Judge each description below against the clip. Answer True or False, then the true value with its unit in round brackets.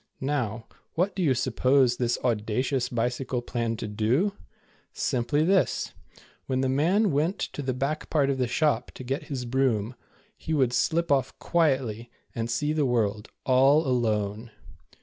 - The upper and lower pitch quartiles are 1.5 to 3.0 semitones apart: False (3.7 semitones)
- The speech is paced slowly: False (155 wpm)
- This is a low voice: True (130 Hz)